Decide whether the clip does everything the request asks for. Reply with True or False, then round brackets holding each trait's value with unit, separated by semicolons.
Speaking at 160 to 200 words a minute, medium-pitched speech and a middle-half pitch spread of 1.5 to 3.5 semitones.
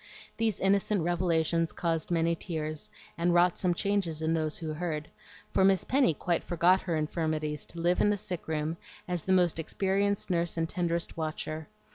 True (175 wpm; 170 Hz; 2.4 semitones)